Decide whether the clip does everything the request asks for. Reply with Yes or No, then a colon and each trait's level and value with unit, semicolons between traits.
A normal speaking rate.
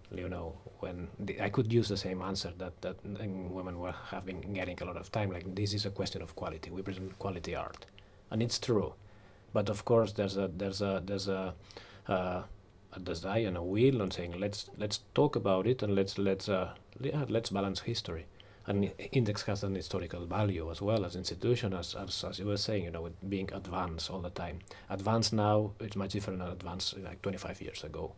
No: fast, 210 wpm